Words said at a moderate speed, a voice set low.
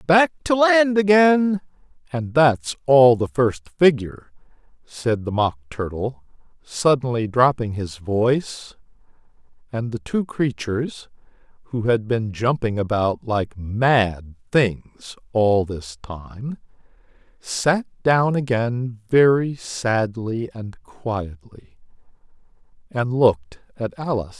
No: slow, 110 wpm; low, 125 Hz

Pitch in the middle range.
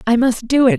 No: high, 245 Hz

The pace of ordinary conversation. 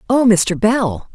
Yes: average, 155 wpm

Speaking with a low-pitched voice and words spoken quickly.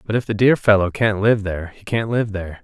Yes: low, 105 Hz; fast, 275 wpm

